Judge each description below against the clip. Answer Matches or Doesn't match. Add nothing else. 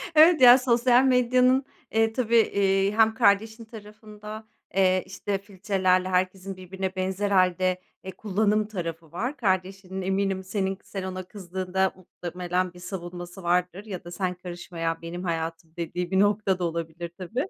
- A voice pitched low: Doesn't match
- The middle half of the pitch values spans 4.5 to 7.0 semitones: Doesn't match